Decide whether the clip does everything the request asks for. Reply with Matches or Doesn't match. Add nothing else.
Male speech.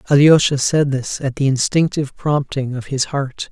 Matches